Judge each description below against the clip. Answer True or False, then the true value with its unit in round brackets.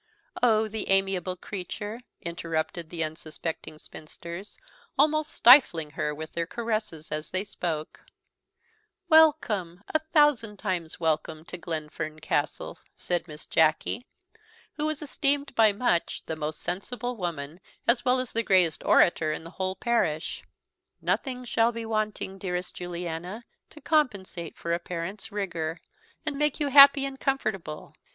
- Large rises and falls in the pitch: True (6.5 semitones)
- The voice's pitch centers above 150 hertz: True (190 Hz)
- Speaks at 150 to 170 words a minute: False (140 wpm)